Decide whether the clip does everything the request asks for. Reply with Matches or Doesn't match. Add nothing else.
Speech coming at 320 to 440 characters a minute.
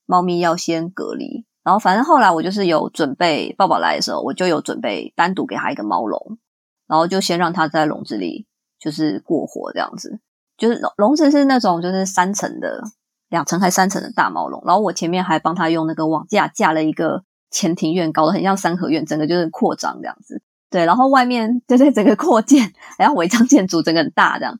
Matches